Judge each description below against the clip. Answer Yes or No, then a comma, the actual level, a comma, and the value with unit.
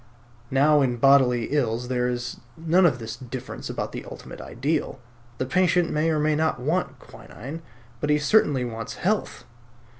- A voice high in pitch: No, medium, 140 Hz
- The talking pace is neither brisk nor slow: Yes, average, 160 wpm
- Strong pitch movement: No, average, 4.3 semitones